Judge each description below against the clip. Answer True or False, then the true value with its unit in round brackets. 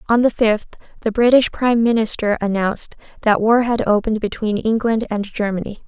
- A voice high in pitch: True (220 Hz)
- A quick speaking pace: False (165 wpm)